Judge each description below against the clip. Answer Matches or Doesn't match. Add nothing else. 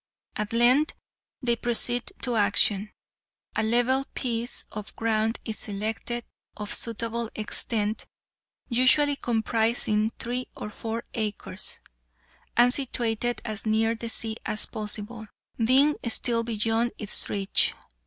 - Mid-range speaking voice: Doesn't match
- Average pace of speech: Doesn't match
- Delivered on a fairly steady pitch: Matches